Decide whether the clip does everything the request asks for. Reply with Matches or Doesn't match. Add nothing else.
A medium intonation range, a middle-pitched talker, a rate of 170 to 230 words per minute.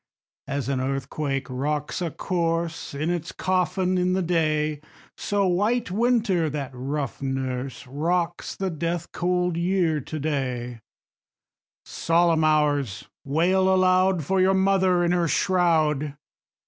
Doesn't match